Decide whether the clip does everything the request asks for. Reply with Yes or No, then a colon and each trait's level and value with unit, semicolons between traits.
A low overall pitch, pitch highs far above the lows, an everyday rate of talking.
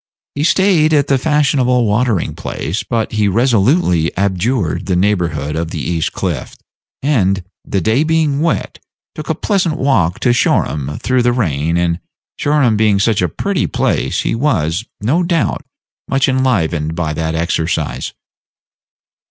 Yes: low, 110 Hz; wide, 8.3 semitones; average, 145 wpm